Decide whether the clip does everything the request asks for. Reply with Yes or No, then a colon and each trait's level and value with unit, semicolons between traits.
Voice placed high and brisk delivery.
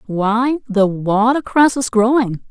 No: high, 230 Hz; slow, 120 wpm